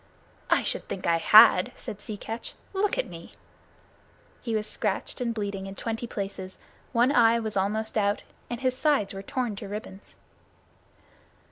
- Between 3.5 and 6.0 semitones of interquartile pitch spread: No, average, 3.0 semitones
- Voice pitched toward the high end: Yes, high, 215 Hz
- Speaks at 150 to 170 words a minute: Yes, average, 160 wpm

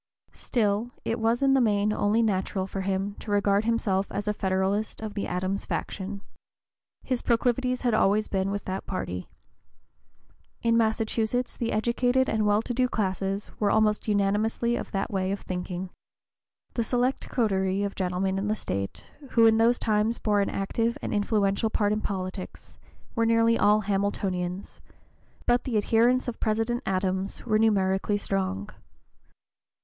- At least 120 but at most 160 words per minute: Yes, average, 155 wpm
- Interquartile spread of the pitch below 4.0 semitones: Yes, average, 2.8 semitones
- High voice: Yes, high, 210 Hz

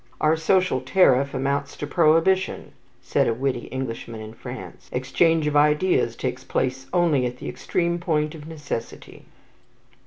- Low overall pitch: No, medium, 145 Hz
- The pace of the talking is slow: No, average, 145 wpm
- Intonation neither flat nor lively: Yes, average, 4.0 semitones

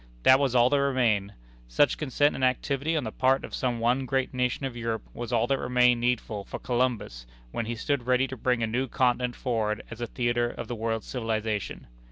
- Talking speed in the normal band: No, fast, 215 wpm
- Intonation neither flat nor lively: No, narrow, 2.2 semitones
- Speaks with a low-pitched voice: Yes, low, 125 Hz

